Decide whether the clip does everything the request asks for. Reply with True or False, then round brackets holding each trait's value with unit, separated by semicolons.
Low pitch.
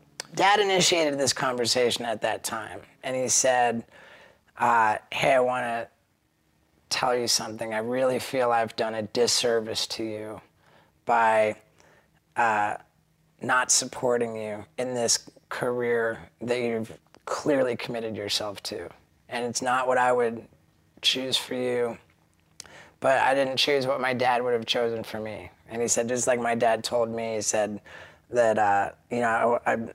True (120 Hz)